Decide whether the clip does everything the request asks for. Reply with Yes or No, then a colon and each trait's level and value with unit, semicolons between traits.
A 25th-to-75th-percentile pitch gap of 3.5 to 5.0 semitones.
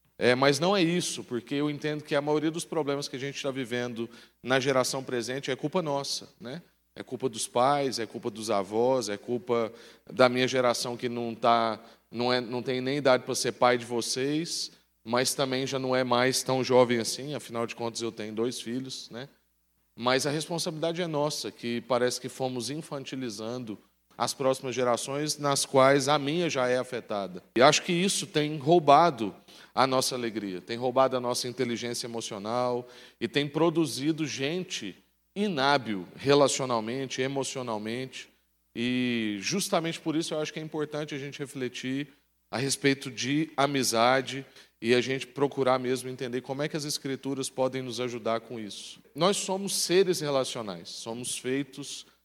No: average, 2.9 semitones